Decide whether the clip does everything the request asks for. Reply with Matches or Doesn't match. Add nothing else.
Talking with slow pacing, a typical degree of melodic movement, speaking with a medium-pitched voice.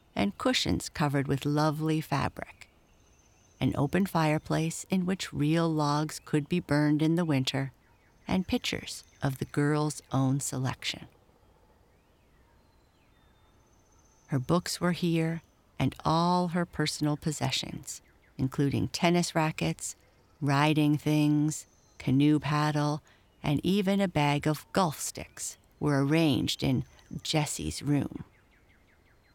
Matches